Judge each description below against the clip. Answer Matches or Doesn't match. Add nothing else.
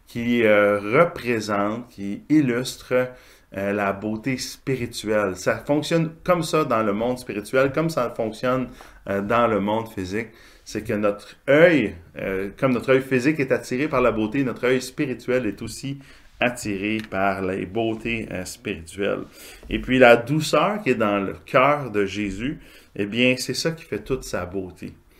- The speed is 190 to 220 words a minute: Doesn't match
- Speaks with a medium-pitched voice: Doesn't match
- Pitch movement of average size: Matches